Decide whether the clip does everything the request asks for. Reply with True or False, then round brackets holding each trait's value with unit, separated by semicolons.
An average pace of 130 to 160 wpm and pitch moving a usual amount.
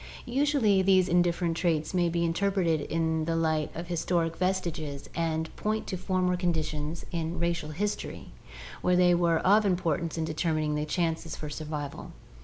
False (155 wpm; 2.3 semitones)